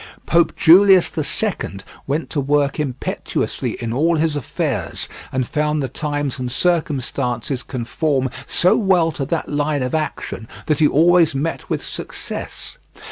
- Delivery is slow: No, average, 145 wpm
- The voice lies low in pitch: No, medium, 150 Hz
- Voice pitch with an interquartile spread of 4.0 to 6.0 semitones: No, average, 3.4 semitones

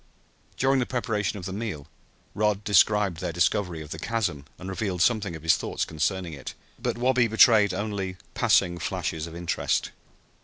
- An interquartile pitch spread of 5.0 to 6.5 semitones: No, average, 4.0 semitones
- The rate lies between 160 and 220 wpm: Yes, average, 165 wpm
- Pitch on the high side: No, very low, 95 Hz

